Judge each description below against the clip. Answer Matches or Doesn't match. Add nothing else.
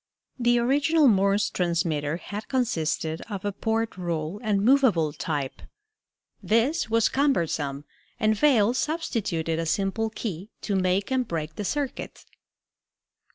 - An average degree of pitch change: Doesn't match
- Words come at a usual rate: Doesn't match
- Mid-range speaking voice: Doesn't match